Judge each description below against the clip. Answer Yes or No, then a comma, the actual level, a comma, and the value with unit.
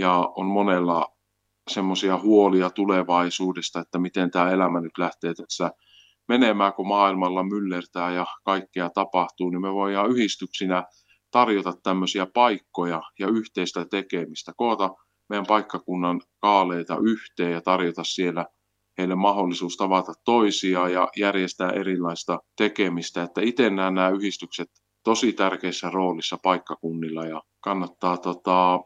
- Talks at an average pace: Yes, average, 120 wpm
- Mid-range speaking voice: No, very low, 95 Hz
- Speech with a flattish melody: Yes, narrow, 2.0 semitones